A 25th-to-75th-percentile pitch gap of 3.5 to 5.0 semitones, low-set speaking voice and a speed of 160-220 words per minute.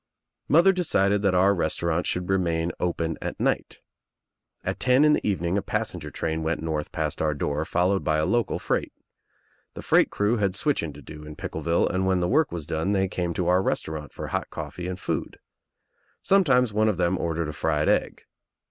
Yes: average, 4.0 semitones; very low, 90 Hz; average, 200 wpm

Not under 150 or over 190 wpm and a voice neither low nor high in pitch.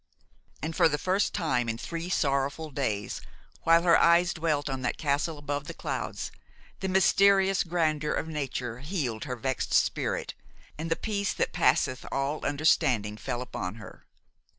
Yes: average, 155 wpm; medium, 150 Hz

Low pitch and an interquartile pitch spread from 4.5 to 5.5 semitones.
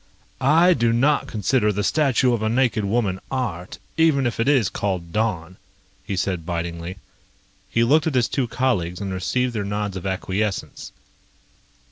Yes: low, 105 Hz; average, 5.2 semitones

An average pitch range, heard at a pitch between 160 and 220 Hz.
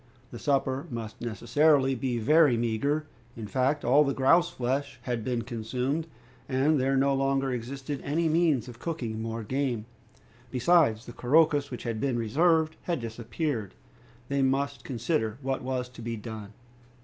No: average, 3.6 semitones; low, 130 Hz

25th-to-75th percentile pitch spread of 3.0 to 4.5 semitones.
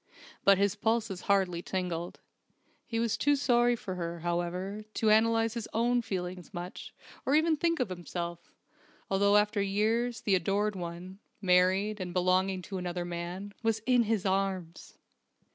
Yes: average, 3.8 semitones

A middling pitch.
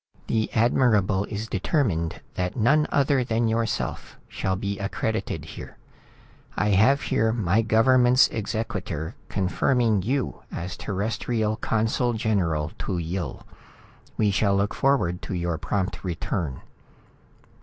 No: low, 105 Hz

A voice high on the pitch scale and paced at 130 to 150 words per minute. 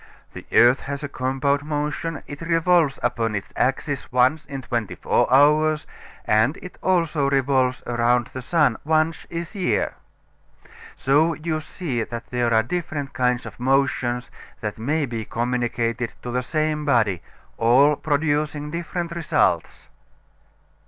No: medium, 140 Hz; average, 140 wpm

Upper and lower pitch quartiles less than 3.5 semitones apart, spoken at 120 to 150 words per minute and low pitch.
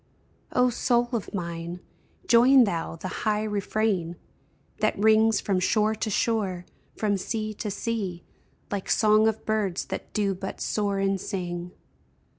No: average, 2.8 semitones; average, 140 wpm; high, 210 Hz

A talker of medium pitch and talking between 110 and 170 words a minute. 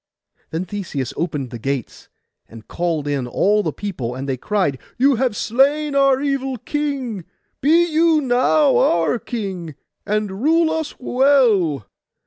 No: high, 215 Hz; average, 140 wpm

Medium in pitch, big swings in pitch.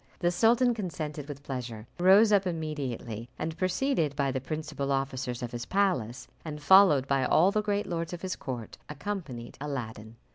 Yes: medium, 150 Hz; wide, 6.1 semitones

